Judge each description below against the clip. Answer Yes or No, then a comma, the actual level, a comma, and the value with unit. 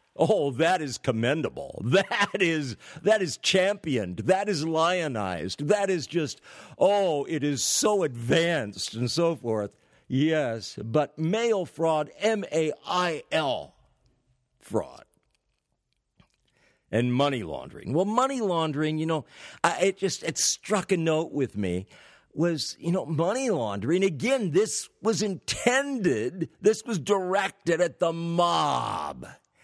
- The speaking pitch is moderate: Yes, medium, 165 Hz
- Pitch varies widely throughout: Yes, wide, 5.7 semitones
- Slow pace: Yes, slow, 125 wpm